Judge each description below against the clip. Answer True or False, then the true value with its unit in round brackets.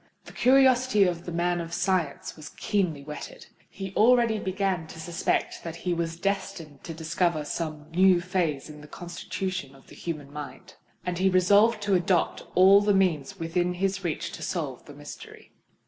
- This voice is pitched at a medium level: True (180 Hz)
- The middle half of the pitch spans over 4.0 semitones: False (3.0 semitones)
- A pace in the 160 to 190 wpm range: True (175 wpm)